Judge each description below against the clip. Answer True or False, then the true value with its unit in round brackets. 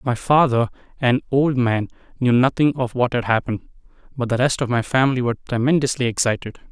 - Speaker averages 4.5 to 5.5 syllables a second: False (6.0 syllables/s)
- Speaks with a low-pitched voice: True (125 Hz)